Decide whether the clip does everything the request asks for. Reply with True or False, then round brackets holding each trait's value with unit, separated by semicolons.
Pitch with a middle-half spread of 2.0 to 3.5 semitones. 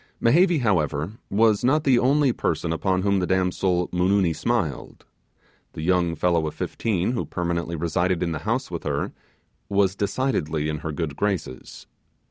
False (4.0 semitones)